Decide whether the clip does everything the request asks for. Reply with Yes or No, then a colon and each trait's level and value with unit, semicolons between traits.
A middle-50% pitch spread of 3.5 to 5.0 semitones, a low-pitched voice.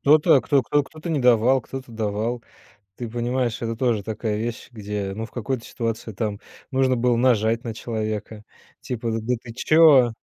No: narrow, 2.6 semitones; low, 120 Hz